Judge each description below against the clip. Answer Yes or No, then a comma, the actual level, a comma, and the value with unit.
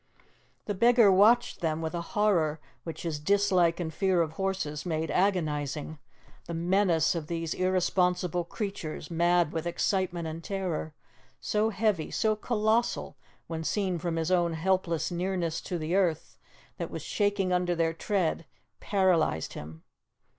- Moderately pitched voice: Yes, medium, 175 Hz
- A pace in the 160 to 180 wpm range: No, average, 145 wpm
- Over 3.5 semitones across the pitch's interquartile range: No, average, 3.0 semitones